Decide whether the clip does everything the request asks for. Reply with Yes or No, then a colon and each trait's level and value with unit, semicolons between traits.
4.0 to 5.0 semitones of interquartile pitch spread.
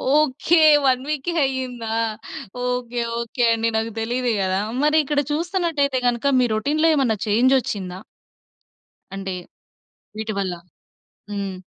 Yes: average, 4.4 semitones